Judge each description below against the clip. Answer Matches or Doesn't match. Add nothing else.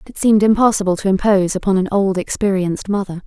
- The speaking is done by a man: Doesn't match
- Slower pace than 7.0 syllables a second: Doesn't match